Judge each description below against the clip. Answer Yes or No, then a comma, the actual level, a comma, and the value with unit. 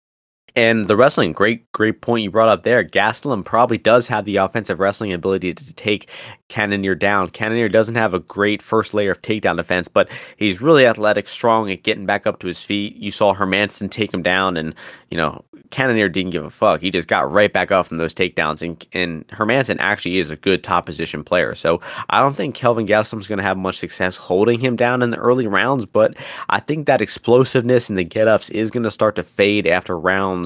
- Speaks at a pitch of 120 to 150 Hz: No, low, 105 Hz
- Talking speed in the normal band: No, fast, 220 wpm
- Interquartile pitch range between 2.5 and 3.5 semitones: Yes, average, 3.1 semitones